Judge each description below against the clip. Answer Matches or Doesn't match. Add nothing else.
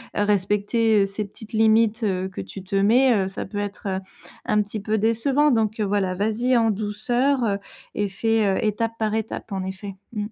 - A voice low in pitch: Doesn't match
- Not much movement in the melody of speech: Matches